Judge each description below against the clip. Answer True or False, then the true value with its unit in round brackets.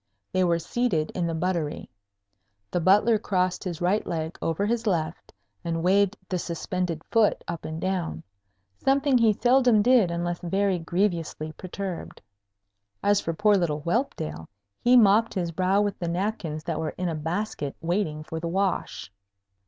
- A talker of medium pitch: True (180 Hz)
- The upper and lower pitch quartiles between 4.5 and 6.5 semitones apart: False (3.8 semitones)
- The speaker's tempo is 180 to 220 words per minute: False (160 wpm)